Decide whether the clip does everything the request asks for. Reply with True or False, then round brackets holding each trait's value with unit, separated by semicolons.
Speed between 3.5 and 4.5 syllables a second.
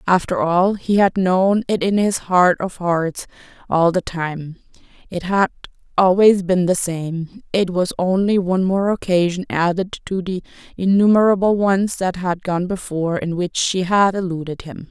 True (4.4 syllables/s)